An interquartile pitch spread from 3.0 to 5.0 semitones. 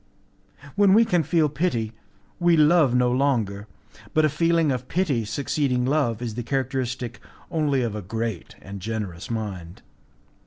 No: wide, 5.5 semitones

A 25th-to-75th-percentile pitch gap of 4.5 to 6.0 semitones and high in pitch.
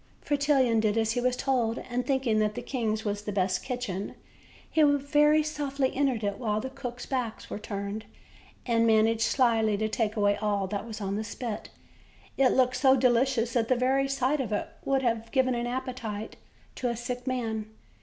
No: average, 3.3 semitones; high, 240 Hz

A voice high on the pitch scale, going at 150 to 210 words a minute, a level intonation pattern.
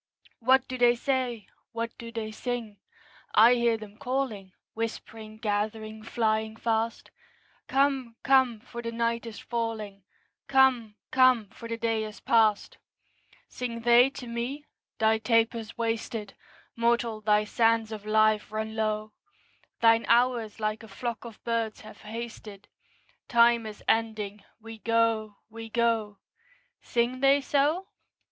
No: high, 230 Hz; slow, 135 wpm; narrow, 1.6 semitones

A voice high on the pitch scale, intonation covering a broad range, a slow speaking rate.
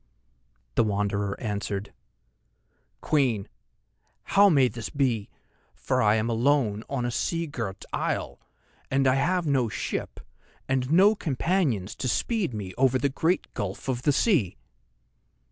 No: low, 130 Hz; wide, 5.7 semitones; slow, 130 wpm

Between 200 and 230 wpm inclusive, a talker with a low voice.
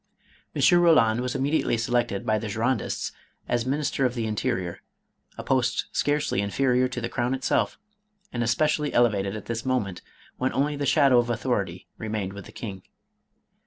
No: average, 160 wpm; low, 120 Hz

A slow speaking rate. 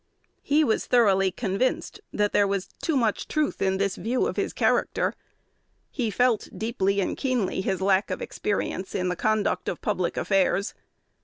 No: average, 165 wpm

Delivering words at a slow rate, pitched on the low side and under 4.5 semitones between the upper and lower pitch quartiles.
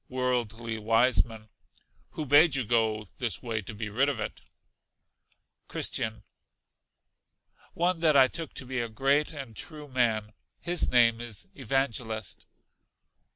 Yes: slow, 130 wpm; low, 120 Hz; average, 3.7 semitones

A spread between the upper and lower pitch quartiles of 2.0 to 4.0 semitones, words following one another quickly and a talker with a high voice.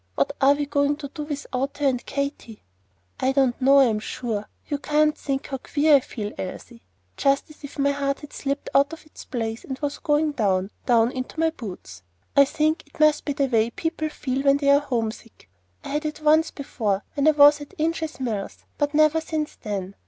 Yes: average, 3.6 semitones; fast, 210 wpm; very high, 280 Hz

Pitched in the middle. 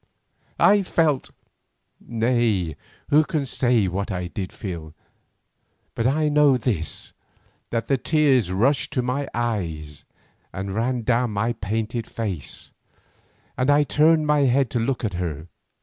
No: low, 120 Hz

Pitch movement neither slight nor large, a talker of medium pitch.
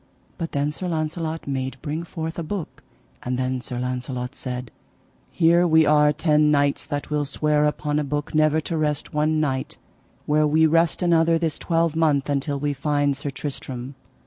No: narrow, 2.3 semitones; medium, 150 Hz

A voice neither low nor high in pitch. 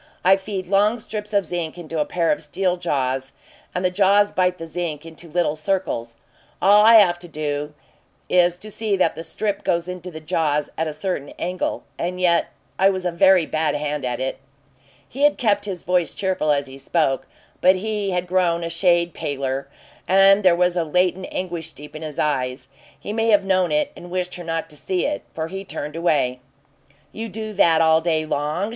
Yes: medium, 175 Hz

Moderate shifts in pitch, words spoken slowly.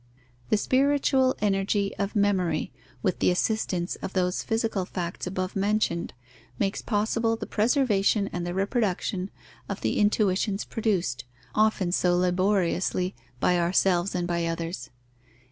Yes: average, 3.0 semitones; slow, 130 wpm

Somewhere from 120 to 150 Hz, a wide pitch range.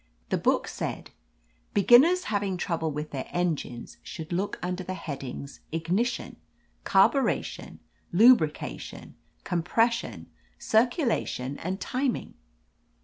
No: medium, 185 Hz; wide, 6.4 semitones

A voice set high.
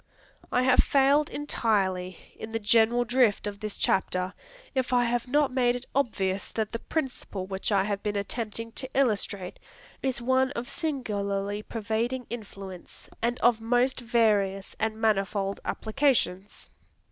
Yes: high, 225 Hz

